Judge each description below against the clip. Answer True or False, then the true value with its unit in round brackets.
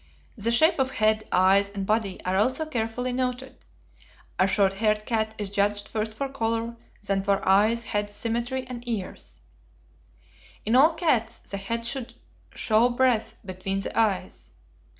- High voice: True (220 Hz)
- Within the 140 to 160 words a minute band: True (150 wpm)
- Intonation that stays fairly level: False (3.4 semitones)